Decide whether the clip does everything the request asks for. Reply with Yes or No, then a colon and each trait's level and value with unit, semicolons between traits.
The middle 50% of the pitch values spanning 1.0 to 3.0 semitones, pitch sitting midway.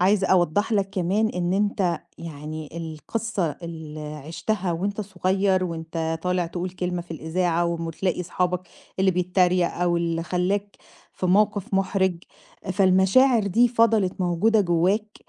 Yes: average, 2.7 semitones; medium, 180 Hz